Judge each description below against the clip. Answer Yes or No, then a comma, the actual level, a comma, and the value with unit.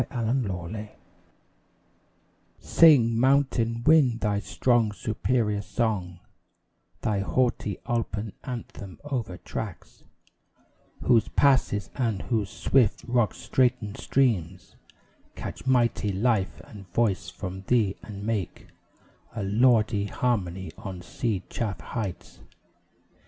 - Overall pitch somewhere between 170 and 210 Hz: No, low, 110 Hz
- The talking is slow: Yes, slow, 100 wpm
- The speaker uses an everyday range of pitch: Yes, average, 3.7 semitones